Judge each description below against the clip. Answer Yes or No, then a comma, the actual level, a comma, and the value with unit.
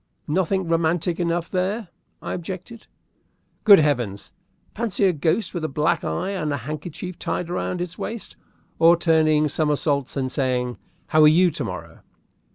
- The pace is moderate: Yes, average, 155 wpm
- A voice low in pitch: No, medium, 165 Hz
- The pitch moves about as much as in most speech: Yes, average, 3.3 semitones